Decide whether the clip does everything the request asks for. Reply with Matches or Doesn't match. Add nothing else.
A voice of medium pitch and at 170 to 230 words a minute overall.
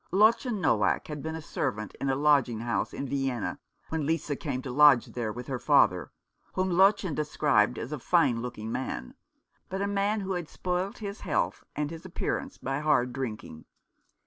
Matches